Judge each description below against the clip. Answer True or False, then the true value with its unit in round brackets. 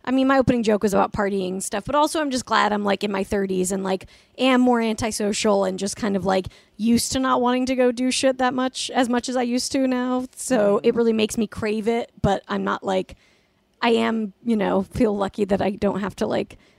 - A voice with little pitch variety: False (4.1 semitones)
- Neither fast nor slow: False (250 wpm)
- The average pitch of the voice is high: True (225 Hz)